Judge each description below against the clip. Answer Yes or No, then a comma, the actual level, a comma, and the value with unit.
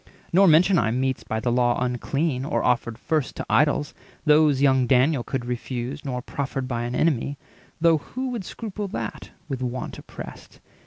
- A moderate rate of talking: Yes, average, 165 wpm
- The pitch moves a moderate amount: Yes, average, 4.0 semitones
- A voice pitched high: No, low, 135 Hz